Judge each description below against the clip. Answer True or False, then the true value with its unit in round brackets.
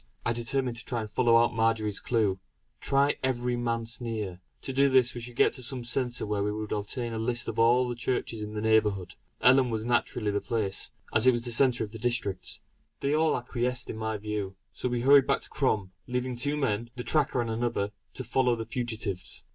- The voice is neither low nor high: False (120 Hz)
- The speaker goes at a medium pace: False (220 wpm)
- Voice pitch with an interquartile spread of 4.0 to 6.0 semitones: False (2.6 semitones)